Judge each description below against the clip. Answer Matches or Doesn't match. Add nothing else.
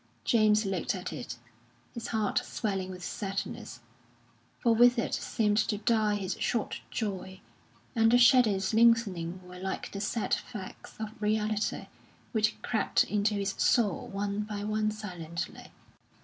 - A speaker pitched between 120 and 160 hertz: Doesn't match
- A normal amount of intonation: Doesn't match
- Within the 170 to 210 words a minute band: Doesn't match